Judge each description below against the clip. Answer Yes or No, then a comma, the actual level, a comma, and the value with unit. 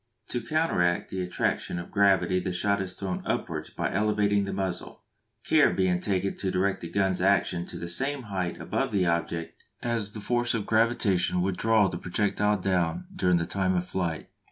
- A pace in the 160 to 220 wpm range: Yes, average, 185 wpm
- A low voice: Yes, very low, 95 Hz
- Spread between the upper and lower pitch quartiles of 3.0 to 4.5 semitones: No, narrow, 2.6 semitones